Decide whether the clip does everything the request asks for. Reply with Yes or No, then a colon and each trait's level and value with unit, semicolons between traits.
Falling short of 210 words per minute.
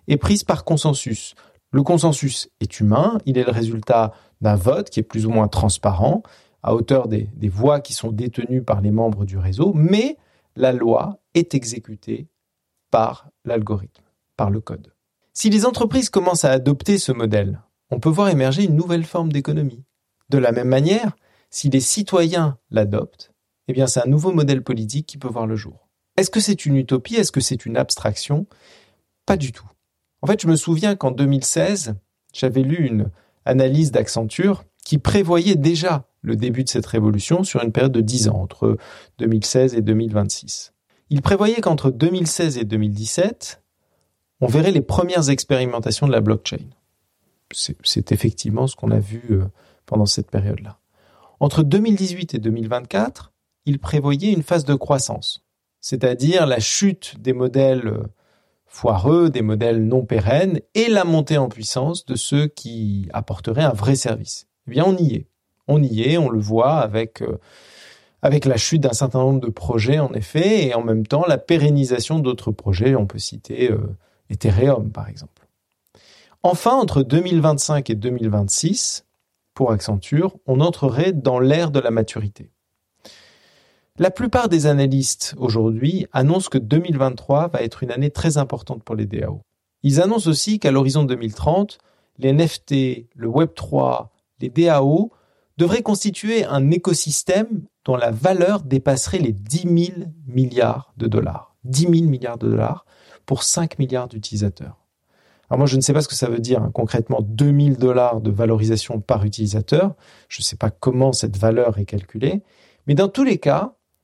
Yes: average, 165 wpm